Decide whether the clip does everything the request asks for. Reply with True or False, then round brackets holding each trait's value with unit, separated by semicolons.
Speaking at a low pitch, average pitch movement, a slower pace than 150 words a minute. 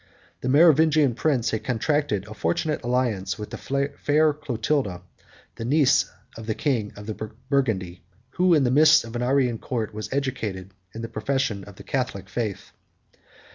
False (125 Hz; 4.9 semitones; 160 wpm)